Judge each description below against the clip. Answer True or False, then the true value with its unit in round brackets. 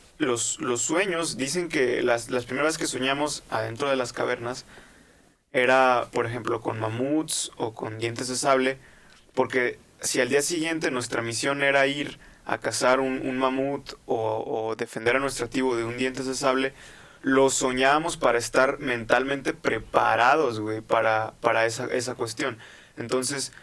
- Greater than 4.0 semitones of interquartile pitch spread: False (2.7 semitones)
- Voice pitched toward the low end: True (130 Hz)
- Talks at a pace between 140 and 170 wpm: True (155 wpm)